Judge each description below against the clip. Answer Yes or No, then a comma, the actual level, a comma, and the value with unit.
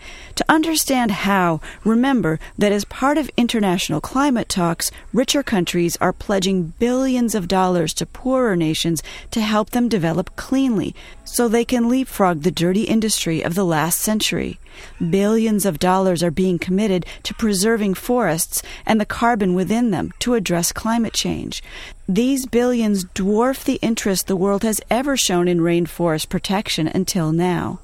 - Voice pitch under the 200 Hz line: No, high, 205 Hz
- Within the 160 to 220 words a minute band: No, average, 150 wpm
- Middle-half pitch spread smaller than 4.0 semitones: No, average, 4.8 semitones